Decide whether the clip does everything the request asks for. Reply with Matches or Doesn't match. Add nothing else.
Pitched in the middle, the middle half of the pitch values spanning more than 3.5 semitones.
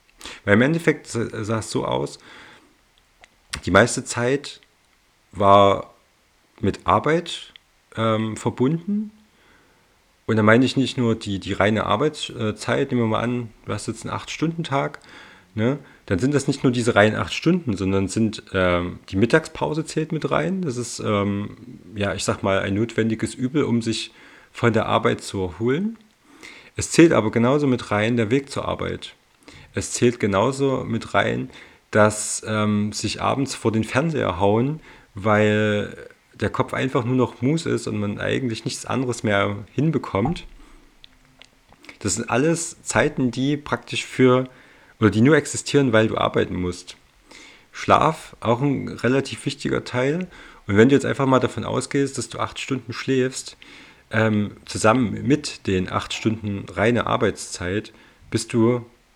Doesn't match